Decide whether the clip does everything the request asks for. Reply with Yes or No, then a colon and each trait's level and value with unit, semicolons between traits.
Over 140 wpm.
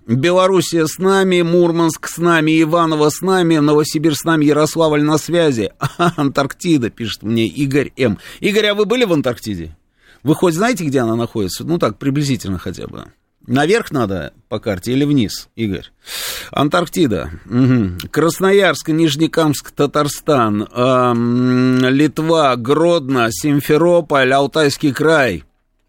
No: average, 125 wpm